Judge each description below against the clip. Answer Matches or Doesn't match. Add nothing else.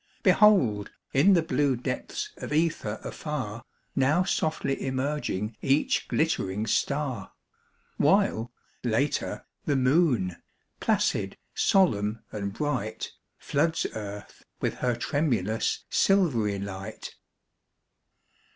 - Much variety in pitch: Matches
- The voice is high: Doesn't match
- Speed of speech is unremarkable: Doesn't match